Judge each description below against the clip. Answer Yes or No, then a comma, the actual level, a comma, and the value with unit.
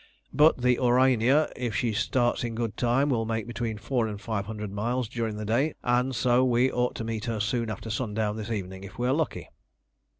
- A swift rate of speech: Yes, fast, 210 wpm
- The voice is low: Yes, low, 115 Hz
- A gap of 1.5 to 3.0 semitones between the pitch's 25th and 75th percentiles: Yes, narrow, 2.4 semitones